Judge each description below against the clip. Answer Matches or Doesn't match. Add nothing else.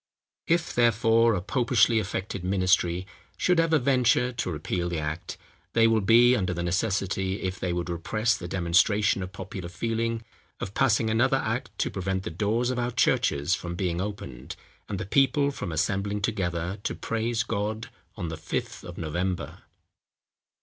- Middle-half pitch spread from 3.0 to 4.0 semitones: Doesn't match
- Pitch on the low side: Matches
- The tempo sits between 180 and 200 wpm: Doesn't match